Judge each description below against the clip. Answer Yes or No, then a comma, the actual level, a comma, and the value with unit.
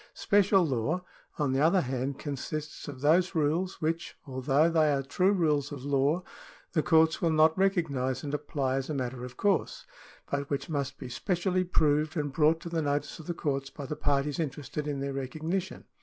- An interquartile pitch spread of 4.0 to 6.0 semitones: No, average, 3.1 semitones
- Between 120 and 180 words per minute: No, average, 190 wpm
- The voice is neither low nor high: Yes, medium, 150 Hz